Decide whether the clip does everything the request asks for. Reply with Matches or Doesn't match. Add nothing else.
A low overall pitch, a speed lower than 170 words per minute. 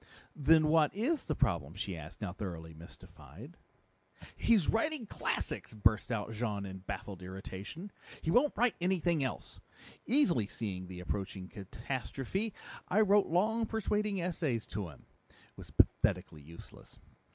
Matches